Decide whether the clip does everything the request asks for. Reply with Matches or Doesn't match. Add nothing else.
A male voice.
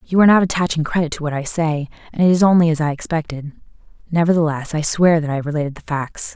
Doesn't match